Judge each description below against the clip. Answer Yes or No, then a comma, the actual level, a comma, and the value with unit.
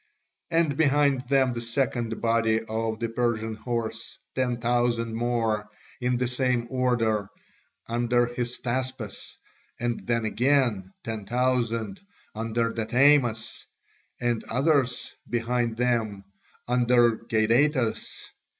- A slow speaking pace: Yes, slow, 105 wpm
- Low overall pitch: Yes, low, 120 Hz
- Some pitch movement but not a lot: No, narrow, 1.8 semitones